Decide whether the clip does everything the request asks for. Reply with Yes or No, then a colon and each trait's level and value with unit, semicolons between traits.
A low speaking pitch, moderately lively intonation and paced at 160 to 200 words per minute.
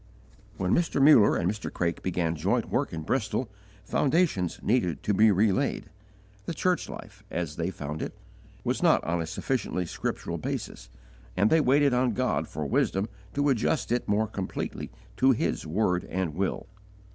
No: low, 100 Hz; wide, 6.4 semitones; average, 165 wpm